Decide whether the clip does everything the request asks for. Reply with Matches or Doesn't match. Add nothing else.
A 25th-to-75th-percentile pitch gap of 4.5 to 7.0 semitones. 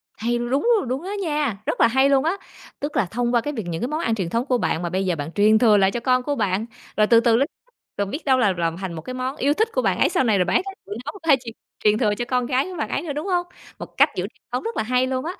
Matches